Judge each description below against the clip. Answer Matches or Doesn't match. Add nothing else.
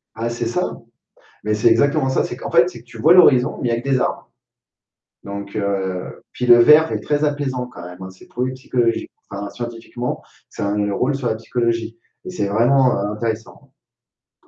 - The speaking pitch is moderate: Doesn't match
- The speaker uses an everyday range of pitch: Matches